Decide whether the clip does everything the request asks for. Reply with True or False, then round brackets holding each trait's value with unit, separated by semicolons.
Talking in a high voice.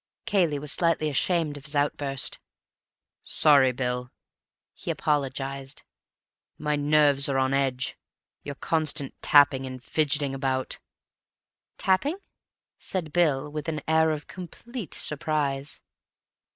False (145 Hz)